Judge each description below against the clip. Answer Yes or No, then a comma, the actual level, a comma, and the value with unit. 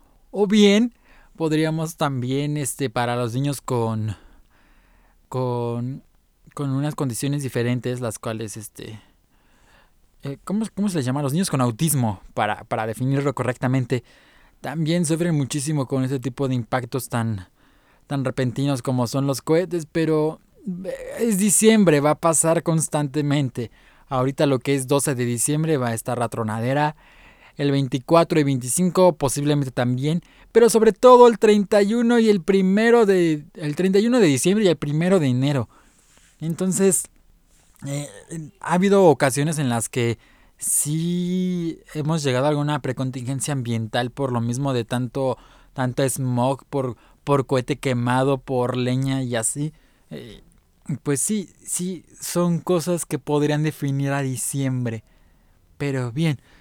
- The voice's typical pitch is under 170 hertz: Yes, medium, 140 Hz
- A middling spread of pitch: Yes, average, 4.5 semitones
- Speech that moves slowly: No, average, 140 wpm